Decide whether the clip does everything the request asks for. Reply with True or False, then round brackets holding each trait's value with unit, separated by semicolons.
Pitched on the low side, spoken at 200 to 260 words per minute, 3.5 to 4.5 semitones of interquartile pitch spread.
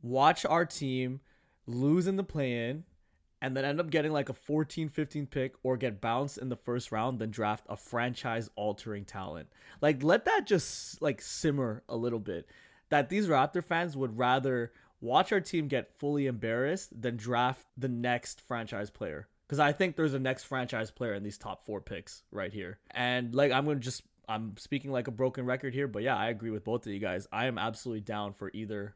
True (125 Hz; 205 wpm; 4.1 semitones)